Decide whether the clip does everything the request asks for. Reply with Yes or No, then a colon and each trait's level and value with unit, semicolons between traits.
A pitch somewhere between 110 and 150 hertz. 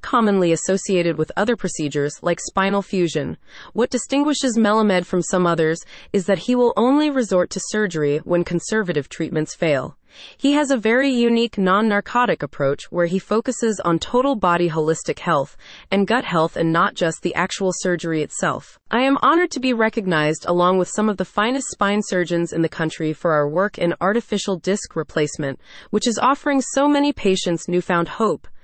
No: high, 190 Hz